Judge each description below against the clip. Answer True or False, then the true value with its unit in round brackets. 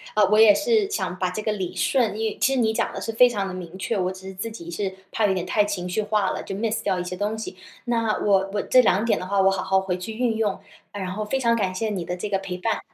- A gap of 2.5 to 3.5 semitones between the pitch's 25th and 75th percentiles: True (2.9 semitones)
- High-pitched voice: True (205 Hz)